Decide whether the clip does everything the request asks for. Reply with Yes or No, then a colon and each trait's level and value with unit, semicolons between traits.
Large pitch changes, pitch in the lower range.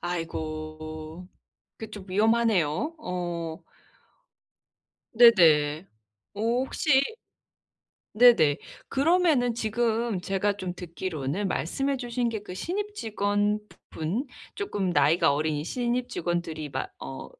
No: wide, 6.7 semitones; high, 200 Hz